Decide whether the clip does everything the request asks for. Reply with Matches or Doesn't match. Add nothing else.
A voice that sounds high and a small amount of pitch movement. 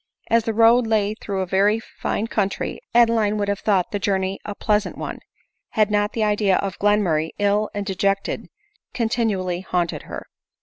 Matches